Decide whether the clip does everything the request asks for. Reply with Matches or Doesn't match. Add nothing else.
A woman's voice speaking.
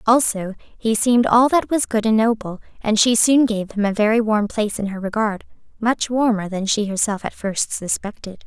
Matches